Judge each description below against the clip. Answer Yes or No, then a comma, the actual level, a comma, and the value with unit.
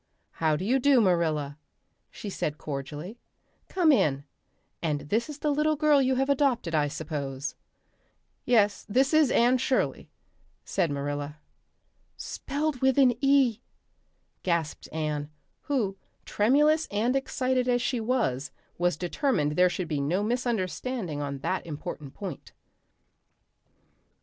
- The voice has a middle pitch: No, high, 205 Hz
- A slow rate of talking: Yes, slow, 130 wpm